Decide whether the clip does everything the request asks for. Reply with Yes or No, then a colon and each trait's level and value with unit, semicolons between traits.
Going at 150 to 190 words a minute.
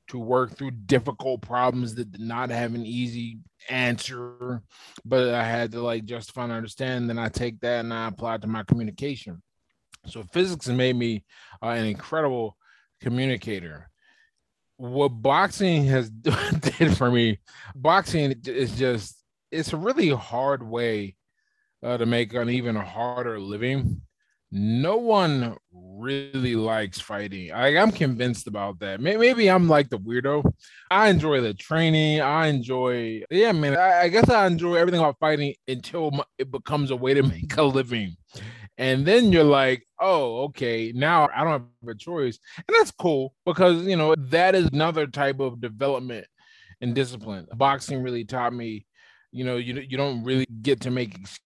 Yes: average, 160 wpm